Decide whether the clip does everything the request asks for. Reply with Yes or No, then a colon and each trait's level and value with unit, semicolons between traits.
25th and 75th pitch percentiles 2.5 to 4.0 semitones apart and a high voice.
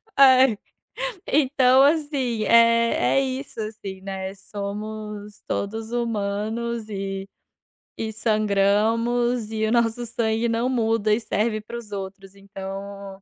Yes: average, 2.8 semitones; high, 220 Hz